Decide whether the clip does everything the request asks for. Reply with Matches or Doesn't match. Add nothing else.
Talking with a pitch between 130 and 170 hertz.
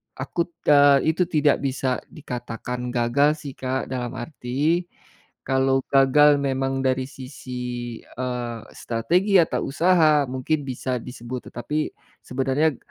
Matches